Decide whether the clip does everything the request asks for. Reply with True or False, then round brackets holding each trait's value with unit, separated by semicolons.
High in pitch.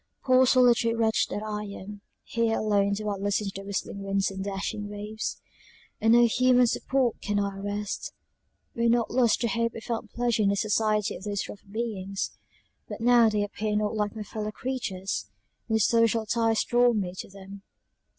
True (215 Hz)